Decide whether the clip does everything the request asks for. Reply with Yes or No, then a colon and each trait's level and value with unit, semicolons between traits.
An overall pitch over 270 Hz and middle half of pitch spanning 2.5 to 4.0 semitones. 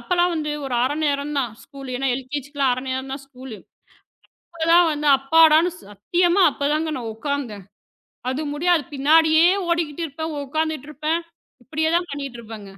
Yes: very high, 290 Hz; average, 3.4 semitones